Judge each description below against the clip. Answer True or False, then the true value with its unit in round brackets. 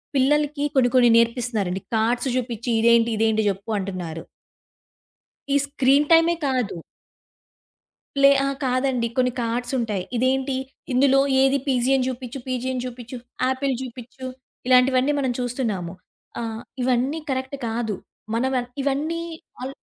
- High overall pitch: True (255 Hz)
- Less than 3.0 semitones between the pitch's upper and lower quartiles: True (2.5 semitones)